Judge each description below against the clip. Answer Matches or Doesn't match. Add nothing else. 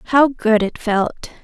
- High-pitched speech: Matches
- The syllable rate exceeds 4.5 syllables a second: Doesn't match